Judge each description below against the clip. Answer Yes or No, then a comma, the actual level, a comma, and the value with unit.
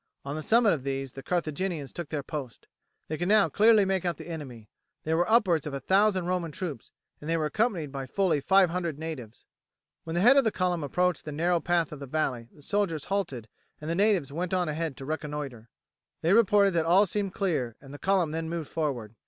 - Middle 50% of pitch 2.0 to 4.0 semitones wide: No, average, 4.5 semitones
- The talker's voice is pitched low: No, medium, 165 Hz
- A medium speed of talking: No, fast, 220 wpm